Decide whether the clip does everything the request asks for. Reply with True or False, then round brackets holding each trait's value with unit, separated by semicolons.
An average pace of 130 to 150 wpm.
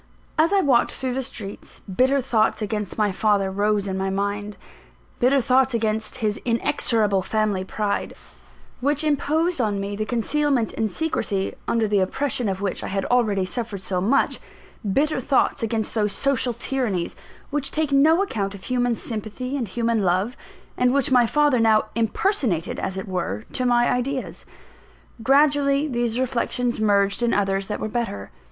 False (165 wpm)